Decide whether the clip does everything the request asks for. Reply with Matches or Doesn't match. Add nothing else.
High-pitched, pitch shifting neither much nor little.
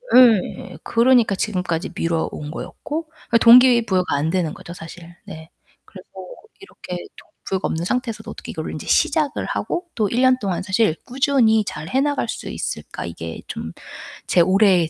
Doesn't match